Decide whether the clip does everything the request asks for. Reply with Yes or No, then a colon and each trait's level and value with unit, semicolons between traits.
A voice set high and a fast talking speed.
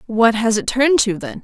Yes: high, 235 Hz; fast, 250 wpm